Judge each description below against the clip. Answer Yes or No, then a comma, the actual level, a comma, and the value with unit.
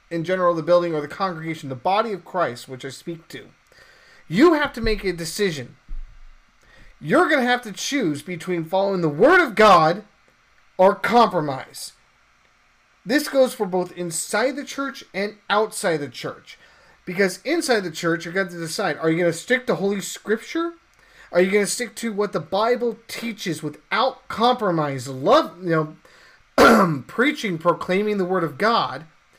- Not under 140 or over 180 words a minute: Yes, average, 175 wpm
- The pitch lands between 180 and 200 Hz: Yes, high, 190 Hz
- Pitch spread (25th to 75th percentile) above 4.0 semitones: Yes, wide, 5.6 semitones